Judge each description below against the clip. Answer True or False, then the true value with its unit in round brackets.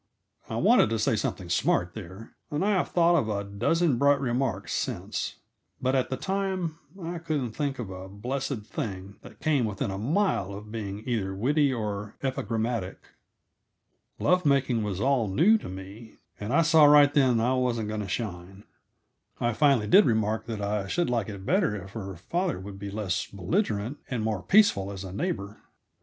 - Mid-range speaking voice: False (115 Hz)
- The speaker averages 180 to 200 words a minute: True (185 wpm)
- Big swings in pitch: True (6.2 semitones)